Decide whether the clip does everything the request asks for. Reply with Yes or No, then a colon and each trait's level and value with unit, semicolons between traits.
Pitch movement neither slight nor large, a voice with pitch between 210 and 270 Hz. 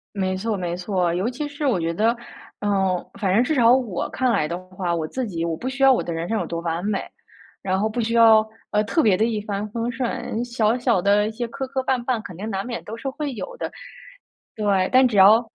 Yes: average, 4.5 semitones; high, 215 Hz